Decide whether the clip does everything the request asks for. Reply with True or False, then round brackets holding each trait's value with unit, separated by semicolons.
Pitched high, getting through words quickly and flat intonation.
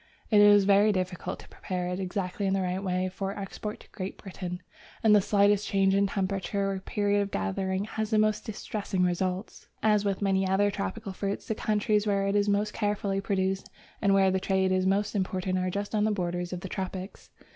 True (195 Hz; 210 wpm; 1.6 semitones)